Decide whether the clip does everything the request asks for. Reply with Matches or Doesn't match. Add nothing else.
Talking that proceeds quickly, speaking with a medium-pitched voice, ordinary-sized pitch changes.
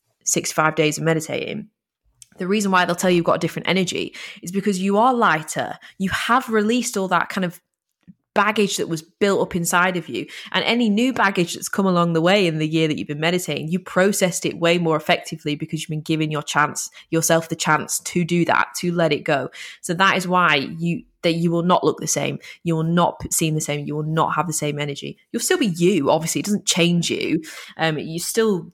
Matches